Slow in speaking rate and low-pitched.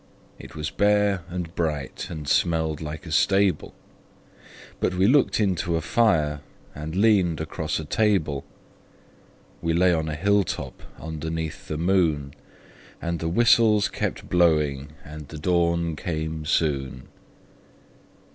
Yes: slow, 130 wpm; very low, 80 Hz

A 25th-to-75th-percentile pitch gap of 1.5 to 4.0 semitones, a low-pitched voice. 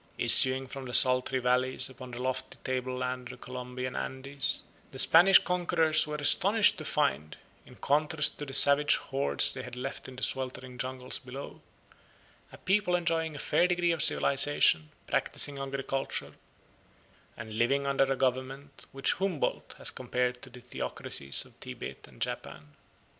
Yes: narrow, 2.4 semitones; low, 130 Hz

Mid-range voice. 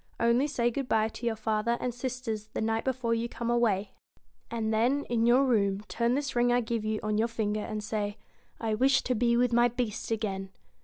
No: high, 230 Hz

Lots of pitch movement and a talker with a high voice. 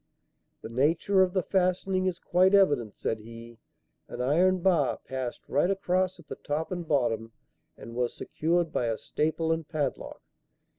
No: wide, 6.7 semitones; medium, 160 Hz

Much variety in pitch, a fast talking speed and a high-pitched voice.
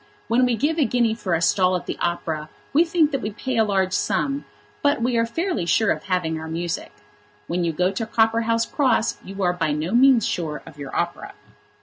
Yes: wide, 6.0 semitones; fast, 220 wpm; high, 210 Hz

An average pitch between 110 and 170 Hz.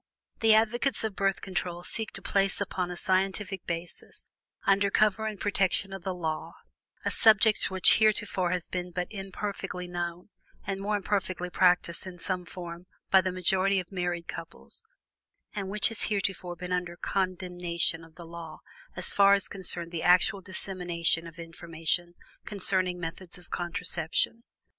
No: medium, 185 Hz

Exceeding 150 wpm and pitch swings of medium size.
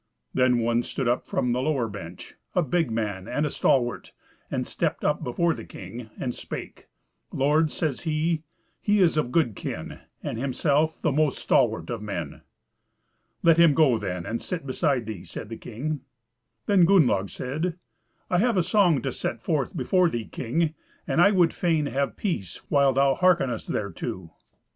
No: average, 170 wpm; wide, 5.9 semitones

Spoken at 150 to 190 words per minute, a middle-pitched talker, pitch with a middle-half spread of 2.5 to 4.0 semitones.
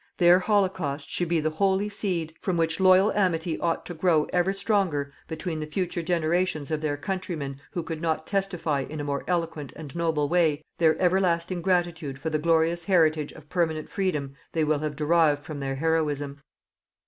Yes: average, 180 wpm; medium, 165 Hz; average, 2.9 semitones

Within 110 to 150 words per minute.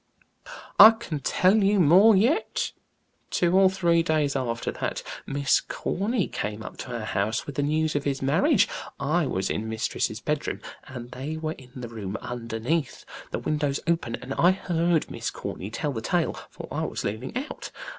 No: average, 175 wpm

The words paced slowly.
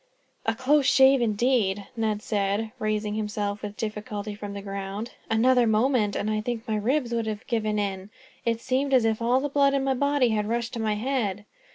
No: average, 200 wpm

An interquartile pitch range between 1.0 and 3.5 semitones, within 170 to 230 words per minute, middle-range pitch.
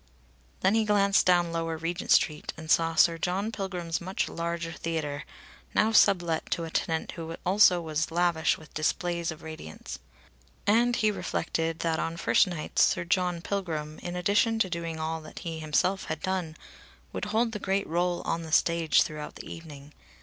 Yes: average, 2.7 semitones; average, 175 wpm; medium, 170 Hz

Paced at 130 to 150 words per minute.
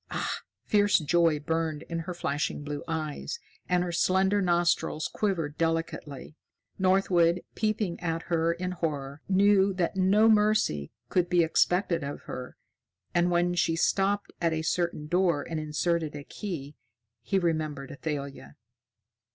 Yes: average, 140 wpm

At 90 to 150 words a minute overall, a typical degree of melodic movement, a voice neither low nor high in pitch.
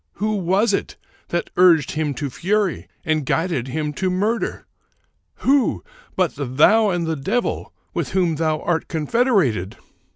Yes: average, 140 wpm; average, 4.9 semitones; medium, 170 Hz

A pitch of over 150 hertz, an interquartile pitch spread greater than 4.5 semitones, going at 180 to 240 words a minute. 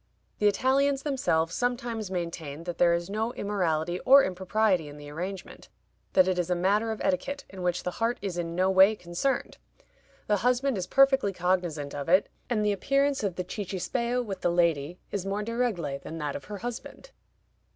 Yes: high, 190 Hz; average, 5.0 semitones; average, 190 wpm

